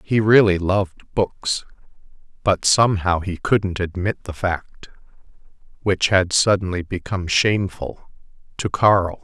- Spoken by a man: Yes, male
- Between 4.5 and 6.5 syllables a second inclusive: No, 4.2 syllables/s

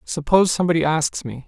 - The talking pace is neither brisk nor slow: Yes, average, 160 wpm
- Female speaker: No, male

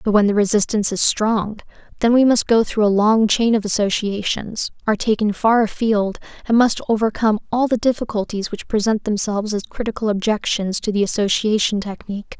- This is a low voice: No, high, 215 Hz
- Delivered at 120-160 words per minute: No, average, 175 wpm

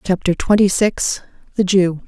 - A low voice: No, high, 190 Hz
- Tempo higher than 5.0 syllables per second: No, 4.4 syllables/s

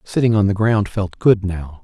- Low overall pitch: Yes, low, 100 Hz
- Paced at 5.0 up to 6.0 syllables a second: No, 4.6 syllables/s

